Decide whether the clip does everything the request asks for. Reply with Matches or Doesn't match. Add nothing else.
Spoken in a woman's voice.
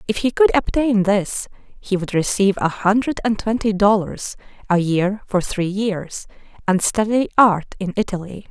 Matches